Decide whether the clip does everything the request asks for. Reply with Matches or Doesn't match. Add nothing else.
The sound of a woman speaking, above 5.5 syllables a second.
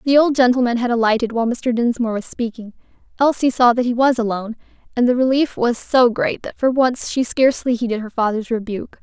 Matches